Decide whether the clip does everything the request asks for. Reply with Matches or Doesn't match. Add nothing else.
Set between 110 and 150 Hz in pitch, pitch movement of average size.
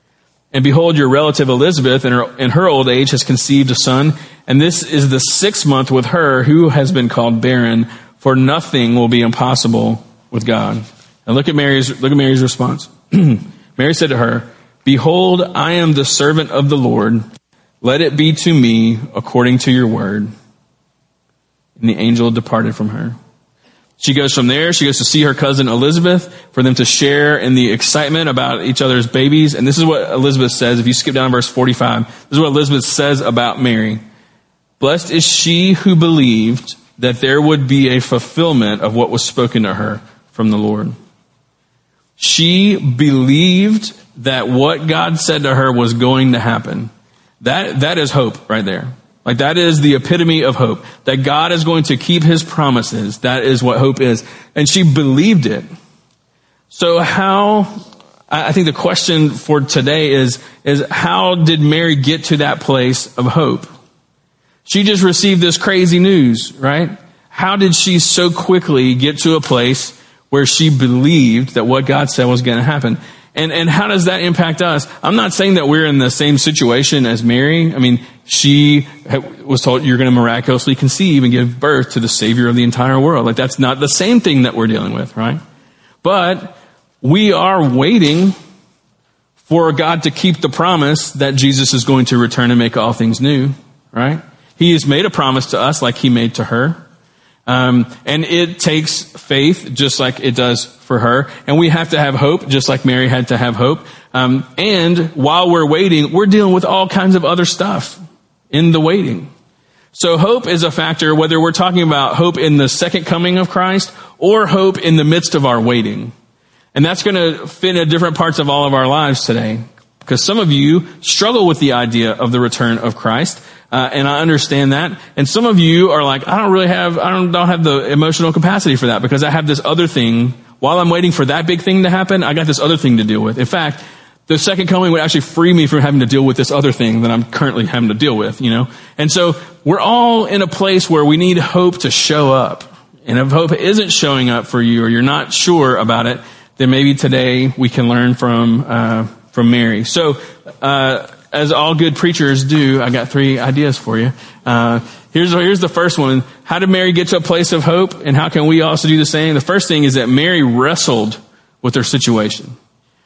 Matches